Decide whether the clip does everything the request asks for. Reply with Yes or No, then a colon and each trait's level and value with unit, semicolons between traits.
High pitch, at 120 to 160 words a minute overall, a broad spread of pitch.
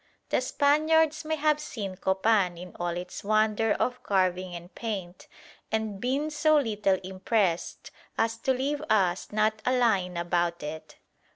Yes: high, 215 Hz; average, 150 wpm; wide, 6.0 semitones